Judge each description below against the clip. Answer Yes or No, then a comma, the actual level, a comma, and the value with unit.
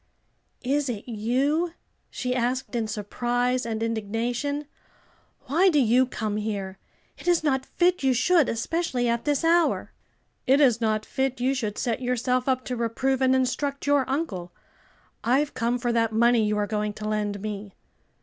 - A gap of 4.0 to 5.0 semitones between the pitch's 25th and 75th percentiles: No, average, 3.6 semitones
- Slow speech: No, average, 165 wpm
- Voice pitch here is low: No, high, 245 Hz